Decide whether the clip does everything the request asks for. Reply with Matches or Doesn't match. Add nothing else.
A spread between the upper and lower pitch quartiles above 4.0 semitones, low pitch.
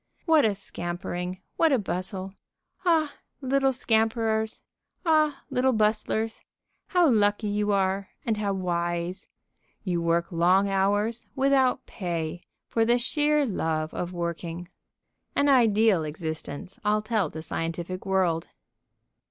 Doesn't match